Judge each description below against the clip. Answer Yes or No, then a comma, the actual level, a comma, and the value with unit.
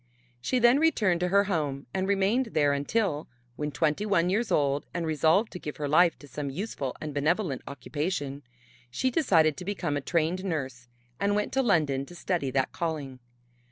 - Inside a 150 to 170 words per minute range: No, average, 185 wpm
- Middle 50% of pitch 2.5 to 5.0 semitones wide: No, wide, 5.5 semitones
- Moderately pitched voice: Yes, medium, 160 Hz